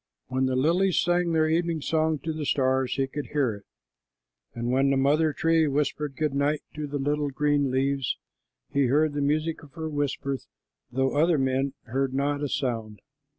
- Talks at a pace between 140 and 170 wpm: No, average, 185 wpm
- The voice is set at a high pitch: No, medium, 145 Hz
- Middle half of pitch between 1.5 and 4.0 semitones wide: Yes, average, 2.7 semitones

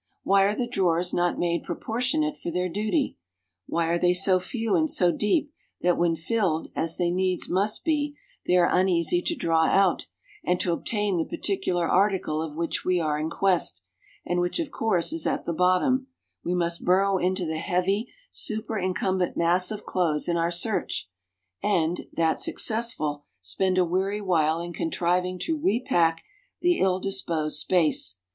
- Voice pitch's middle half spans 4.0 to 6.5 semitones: No, average, 3.4 semitones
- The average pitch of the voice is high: No, medium, 180 Hz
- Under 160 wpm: No, average, 170 wpm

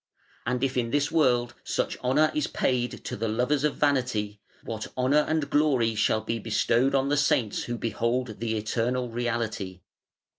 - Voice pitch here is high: No, low, 125 Hz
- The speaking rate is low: No, average, 170 wpm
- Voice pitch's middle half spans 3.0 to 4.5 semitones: Yes, average, 3.4 semitones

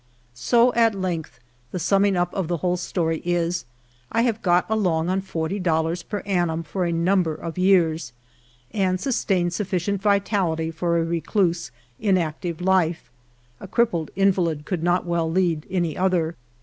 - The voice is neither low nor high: Yes, medium, 175 Hz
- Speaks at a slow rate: No, average, 155 wpm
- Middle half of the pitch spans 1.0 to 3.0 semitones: Yes, average, 2.7 semitones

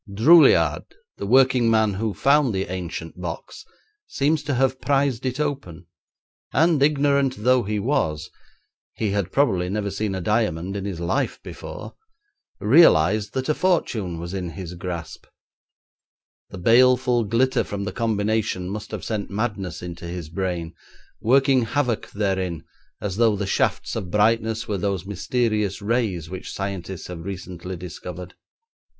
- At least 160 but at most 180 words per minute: No, average, 145 wpm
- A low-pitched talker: Yes, low, 105 Hz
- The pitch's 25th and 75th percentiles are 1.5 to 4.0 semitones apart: No, wide, 5.5 semitones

